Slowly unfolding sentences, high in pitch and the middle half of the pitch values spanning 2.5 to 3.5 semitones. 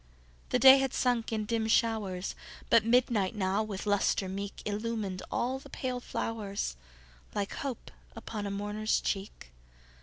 Yes: slow, 125 wpm; high, 210 Hz; average, 2.8 semitones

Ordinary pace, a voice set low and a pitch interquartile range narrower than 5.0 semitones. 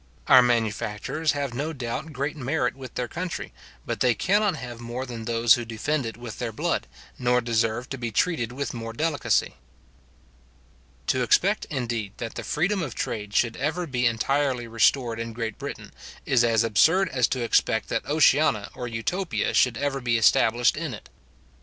Yes: average, 180 wpm; low, 125 Hz; average, 3.8 semitones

